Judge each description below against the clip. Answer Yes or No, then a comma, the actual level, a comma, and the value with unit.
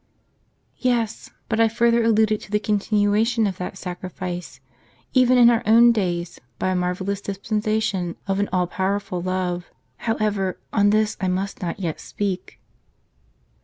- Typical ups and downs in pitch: Yes, average, 3.1 semitones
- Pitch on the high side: Yes, high, 205 Hz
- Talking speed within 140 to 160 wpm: Yes, average, 150 wpm